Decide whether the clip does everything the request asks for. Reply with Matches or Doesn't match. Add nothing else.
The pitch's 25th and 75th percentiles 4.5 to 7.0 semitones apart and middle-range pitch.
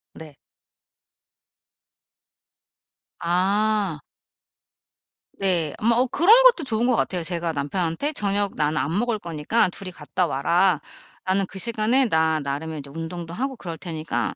Matches